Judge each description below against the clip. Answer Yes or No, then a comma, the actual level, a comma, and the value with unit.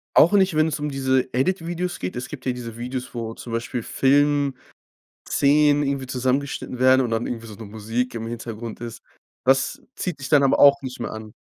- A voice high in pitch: No, low, 130 Hz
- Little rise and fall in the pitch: No, average, 3.3 semitones